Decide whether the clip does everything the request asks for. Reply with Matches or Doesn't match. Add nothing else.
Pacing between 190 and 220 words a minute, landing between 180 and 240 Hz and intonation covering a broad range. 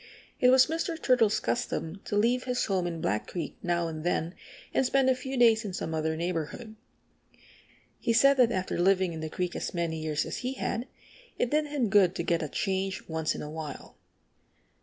Matches